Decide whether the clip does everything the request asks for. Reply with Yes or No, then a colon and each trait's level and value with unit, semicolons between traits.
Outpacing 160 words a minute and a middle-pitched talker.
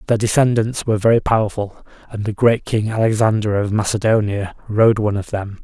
No: average, 170 wpm; low, 110 Hz